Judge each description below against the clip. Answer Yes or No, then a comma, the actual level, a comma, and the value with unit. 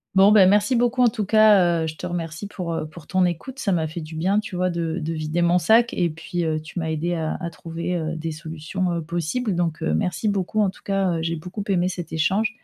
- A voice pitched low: No, medium, 175 Hz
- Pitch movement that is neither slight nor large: Yes, average, 3.3 semitones